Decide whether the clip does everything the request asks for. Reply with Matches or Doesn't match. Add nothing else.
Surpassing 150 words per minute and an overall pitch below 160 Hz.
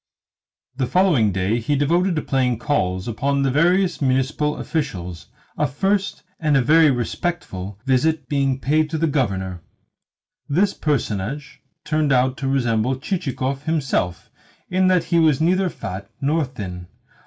Doesn't match